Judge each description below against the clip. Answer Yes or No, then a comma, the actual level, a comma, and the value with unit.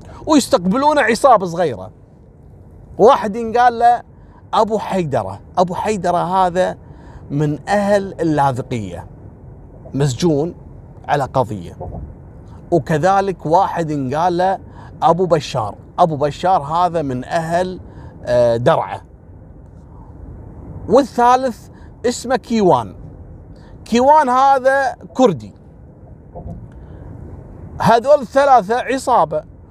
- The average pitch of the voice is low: No, medium, 170 Hz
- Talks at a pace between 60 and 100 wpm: Yes, average, 75 wpm